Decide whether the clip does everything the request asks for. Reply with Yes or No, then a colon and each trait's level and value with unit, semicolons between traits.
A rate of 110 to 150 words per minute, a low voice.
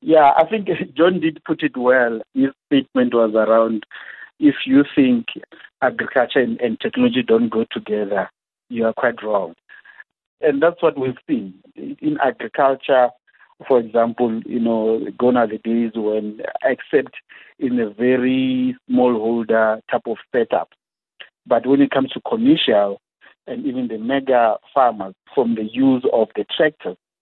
Yes: average, 145 wpm; low, 130 Hz